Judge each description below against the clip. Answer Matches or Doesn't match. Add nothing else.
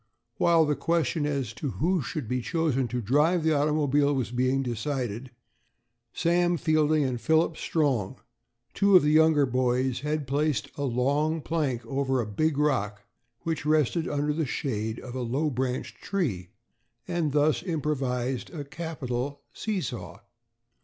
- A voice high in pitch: Doesn't match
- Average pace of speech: Matches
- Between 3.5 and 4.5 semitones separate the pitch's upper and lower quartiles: Matches